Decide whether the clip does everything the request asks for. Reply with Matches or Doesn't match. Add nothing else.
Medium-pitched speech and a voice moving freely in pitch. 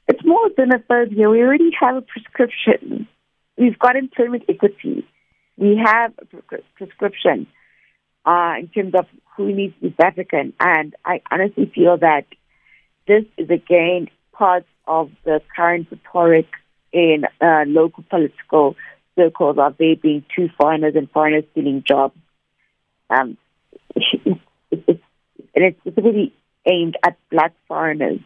Matches